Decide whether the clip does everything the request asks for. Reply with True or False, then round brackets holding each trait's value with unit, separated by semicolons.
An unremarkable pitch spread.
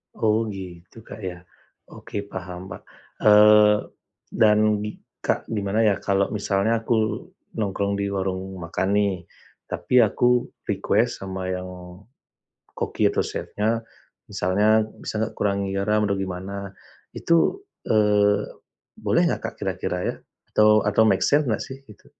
False (1.9 semitones)